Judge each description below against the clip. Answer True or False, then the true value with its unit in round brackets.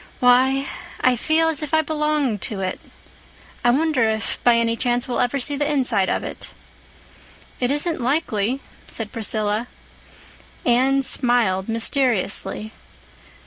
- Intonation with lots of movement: False (3.9 semitones)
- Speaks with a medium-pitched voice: False (245 Hz)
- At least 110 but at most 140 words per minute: True (135 wpm)